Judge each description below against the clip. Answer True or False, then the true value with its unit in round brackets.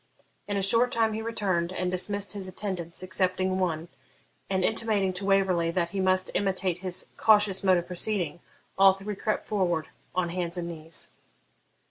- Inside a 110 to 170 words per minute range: True (165 wpm)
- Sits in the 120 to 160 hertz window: False (185 Hz)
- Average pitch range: False (2.3 semitones)